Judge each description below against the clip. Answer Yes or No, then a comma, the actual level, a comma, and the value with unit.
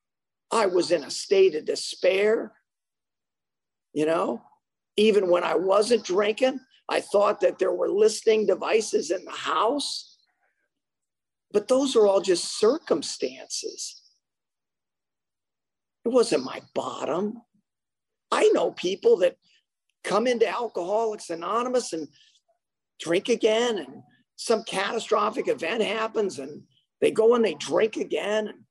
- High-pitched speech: Yes, high, 225 Hz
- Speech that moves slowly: Yes, slow, 120 wpm